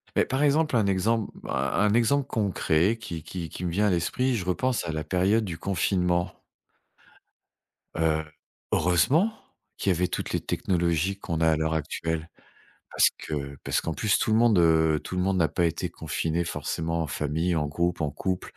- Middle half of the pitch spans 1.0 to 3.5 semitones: No, average, 4.3 semitones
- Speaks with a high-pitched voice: No, very low, 90 Hz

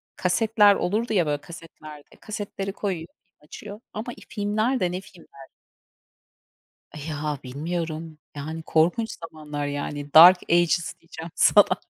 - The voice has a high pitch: No, medium, 170 Hz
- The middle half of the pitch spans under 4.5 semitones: No, average, 5.0 semitones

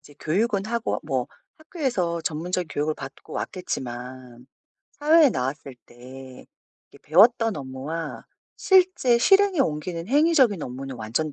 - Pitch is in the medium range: Yes, medium, 165 Hz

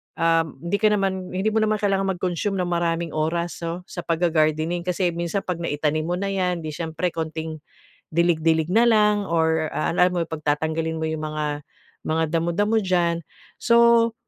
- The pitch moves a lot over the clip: No, average, 2.9 semitones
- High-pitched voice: No, medium, 170 Hz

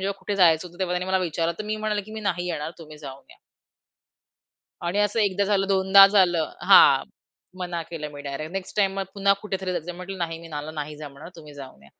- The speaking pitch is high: No, medium, 180 Hz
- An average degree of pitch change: Yes, average, 3.9 semitones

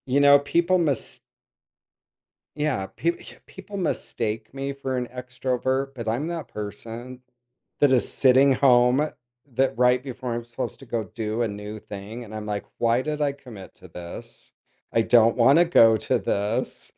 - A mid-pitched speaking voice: No, low, 125 Hz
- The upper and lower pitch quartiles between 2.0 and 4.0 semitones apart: Yes, average, 3.7 semitones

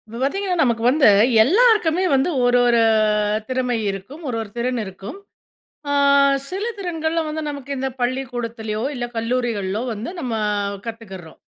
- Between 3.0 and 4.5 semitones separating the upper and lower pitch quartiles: No, average, 5.2 semitones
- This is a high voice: Yes, high, 245 Hz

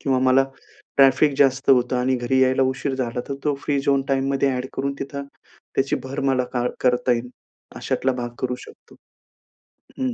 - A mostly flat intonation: Yes, narrow, 1.3 semitones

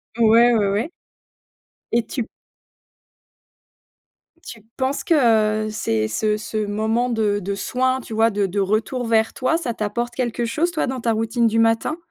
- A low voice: No, high, 225 Hz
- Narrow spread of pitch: Yes, narrow, 2.2 semitones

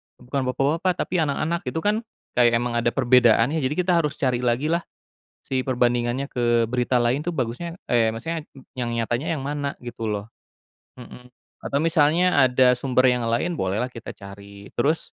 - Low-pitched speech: Yes, low, 125 Hz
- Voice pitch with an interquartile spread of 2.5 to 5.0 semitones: Yes, average, 3.9 semitones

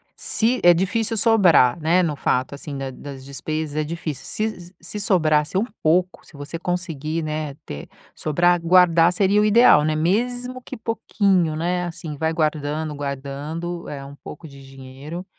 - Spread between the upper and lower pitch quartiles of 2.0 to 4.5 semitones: Yes, average, 3.8 semitones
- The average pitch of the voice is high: No, medium, 165 Hz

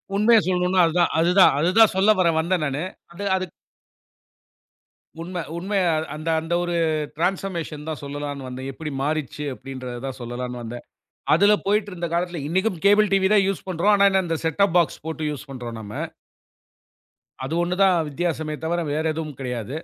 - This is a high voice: No, medium, 165 Hz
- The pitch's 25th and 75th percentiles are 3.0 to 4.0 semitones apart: No, average, 4.6 semitones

